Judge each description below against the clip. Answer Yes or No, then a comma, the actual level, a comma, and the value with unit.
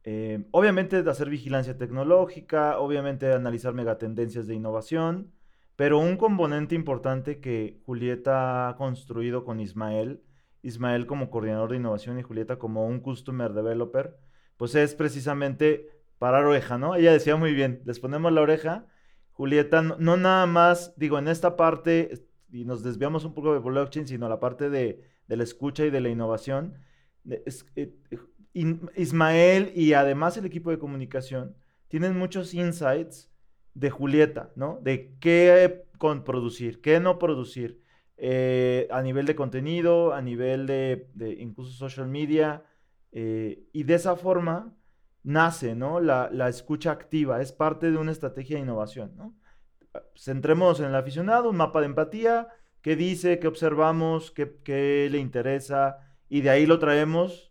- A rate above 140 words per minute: Yes, average, 155 wpm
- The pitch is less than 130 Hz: No, medium, 140 Hz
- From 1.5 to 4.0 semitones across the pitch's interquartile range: No, average, 4.6 semitones